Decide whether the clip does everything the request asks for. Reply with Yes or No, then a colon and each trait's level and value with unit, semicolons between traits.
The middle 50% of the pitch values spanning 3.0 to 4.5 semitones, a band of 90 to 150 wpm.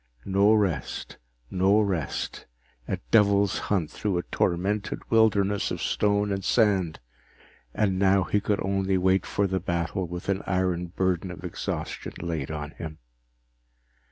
No: narrow, 2.5 semitones; average, 140 wpm